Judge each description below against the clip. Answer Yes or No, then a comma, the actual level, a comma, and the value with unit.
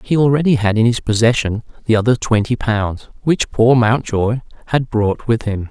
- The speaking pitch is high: No, low, 115 Hz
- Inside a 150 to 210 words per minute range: Yes, average, 180 wpm